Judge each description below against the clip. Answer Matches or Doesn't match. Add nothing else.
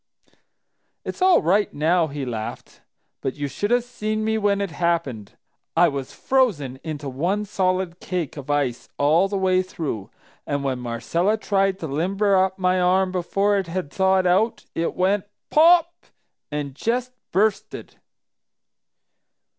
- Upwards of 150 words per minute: Doesn't match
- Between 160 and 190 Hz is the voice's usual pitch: Matches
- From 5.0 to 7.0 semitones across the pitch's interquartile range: Matches